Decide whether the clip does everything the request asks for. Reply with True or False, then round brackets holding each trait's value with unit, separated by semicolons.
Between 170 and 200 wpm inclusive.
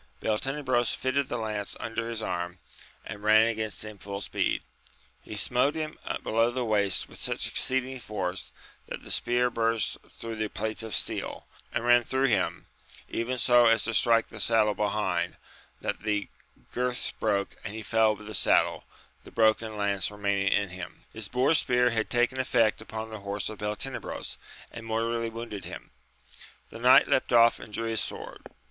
True (175 wpm)